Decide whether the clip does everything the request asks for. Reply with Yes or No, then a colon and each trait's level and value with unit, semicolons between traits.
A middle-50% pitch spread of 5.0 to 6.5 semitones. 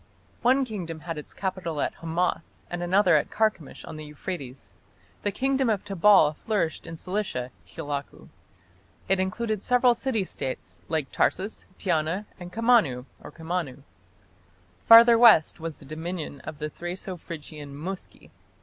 Yes: average, 5.3 semitones